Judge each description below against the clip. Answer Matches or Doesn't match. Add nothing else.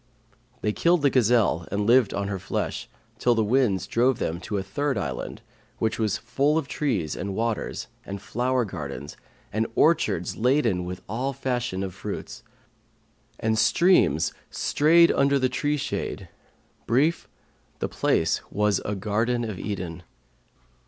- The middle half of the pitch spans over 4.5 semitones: Matches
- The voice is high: Doesn't match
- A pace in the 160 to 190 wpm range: Doesn't match